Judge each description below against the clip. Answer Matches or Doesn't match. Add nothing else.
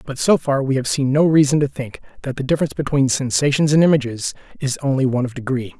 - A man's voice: Matches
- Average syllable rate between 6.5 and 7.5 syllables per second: Matches